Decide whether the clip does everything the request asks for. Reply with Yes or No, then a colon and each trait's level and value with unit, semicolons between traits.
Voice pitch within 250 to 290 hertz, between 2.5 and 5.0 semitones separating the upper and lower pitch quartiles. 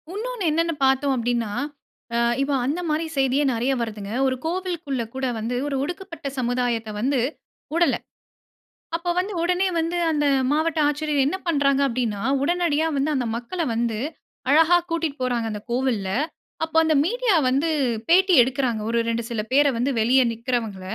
No: very high, 275 Hz; wide, 5.5 semitones